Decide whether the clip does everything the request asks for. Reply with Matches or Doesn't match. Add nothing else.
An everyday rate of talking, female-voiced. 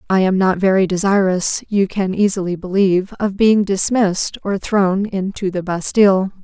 Matches